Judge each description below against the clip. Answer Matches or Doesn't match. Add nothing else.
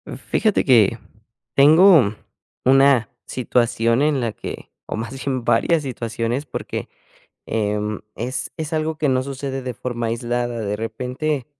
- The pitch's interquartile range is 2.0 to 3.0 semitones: Doesn't match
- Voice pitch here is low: Matches